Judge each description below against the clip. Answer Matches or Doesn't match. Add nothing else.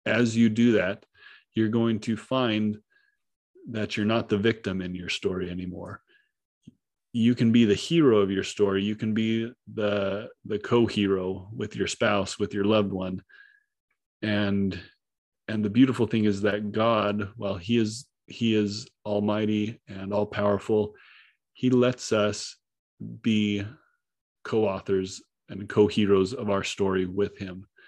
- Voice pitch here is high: Doesn't match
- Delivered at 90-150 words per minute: Matches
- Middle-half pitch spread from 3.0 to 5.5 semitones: Doesn't match